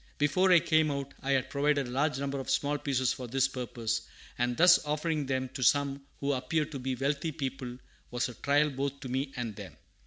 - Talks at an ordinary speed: No, fast, 215 wpm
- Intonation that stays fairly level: Yes, narrow, 2.2 semitones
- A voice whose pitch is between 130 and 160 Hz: Yes, medium, 140 Hz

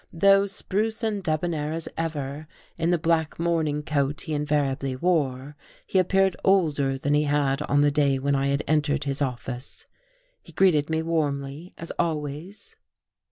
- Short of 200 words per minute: Yes, average, 160 wpm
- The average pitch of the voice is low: No, medium, 150 Hz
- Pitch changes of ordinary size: Yes, average, 3.1 semitones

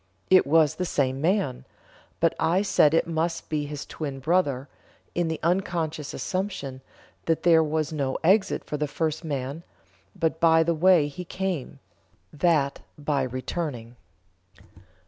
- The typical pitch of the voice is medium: Yes, medium, 160 Hz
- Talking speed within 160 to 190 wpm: No, average, 145 wpm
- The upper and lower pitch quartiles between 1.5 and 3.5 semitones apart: Yes, average, 3.2 semitones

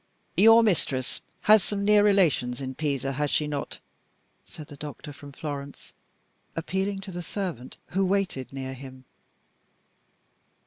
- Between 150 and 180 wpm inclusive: No, slow, 135 wpm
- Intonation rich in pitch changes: Yes, wide, 6.2 semitones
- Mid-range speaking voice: Yes, medium, 150 Hz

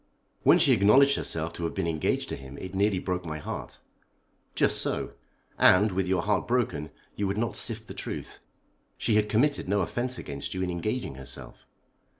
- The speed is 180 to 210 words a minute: Yes, average, 185 wpm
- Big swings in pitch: No, average, 4.3 semitones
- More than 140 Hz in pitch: No, very low, 95 Hz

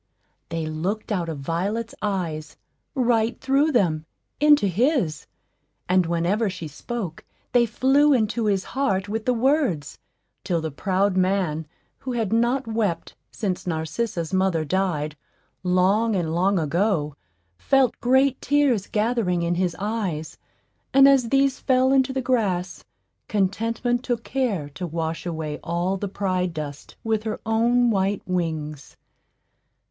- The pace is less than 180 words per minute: Yes, slow, 135 wpm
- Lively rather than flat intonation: Yes, wide, 5.8 semitones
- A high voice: Yes, high, 195 Hz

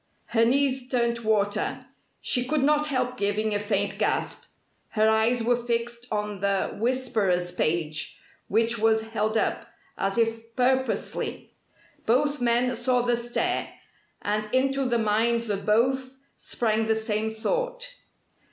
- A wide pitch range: No, average, 2.7 semitones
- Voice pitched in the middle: No, high, 230 Hz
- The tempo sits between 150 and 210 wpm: No, average, 140 wpm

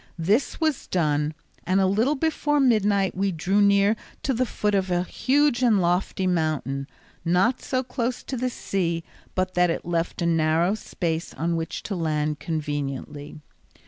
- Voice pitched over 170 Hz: Yes, medium, 185 Hz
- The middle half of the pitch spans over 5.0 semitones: Yes, wide, 5.4 semitones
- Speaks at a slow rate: No, average, 165 wpm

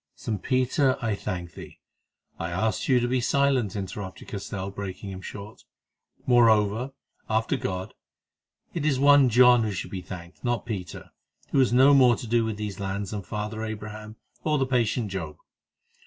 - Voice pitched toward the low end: Yes, low, 110 Hz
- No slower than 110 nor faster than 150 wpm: No, average, 170 wpm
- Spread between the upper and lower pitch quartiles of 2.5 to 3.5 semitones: No, average, 4.1 semitones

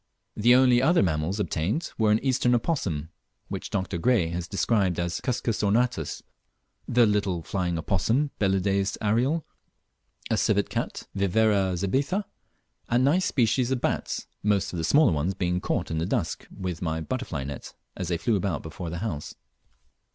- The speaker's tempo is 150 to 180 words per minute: Yes, average, 160 wpm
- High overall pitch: No, low, 100 Hz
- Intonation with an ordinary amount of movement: No, wide, 5.7 semitones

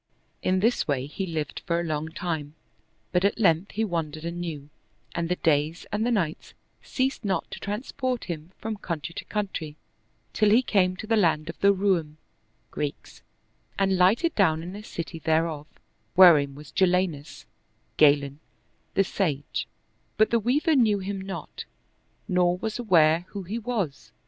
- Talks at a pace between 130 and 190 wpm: Yes, average, 160 wpm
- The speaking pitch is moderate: Yes, medium, 180 Hz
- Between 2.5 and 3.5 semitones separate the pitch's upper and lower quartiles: No, average, 4.6 semitones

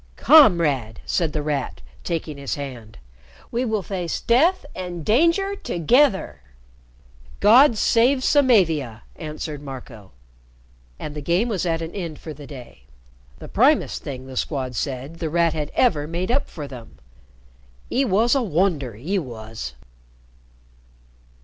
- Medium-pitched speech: Yes, medium, 165 Hz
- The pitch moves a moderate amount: No, wide, 7.6 semitones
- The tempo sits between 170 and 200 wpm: No, slow, 135 wpm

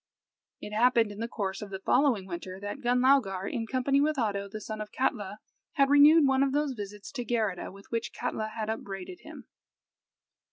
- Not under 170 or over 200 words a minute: Yes, average, 190 wpm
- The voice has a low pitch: No, high, 225 Hz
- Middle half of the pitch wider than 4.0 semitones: Yes, average, 4.8 semitones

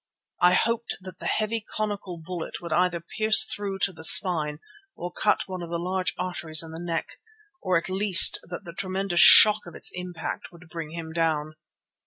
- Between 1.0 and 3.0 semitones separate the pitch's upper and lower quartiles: Yes, narrow, 2.5 semitones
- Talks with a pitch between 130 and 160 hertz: No, medium, 180 Hz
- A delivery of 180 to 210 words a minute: Yes, average, 190 wpm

